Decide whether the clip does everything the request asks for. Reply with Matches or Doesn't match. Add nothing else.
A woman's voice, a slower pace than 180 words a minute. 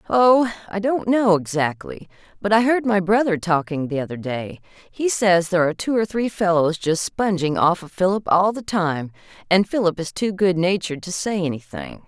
Doesn't match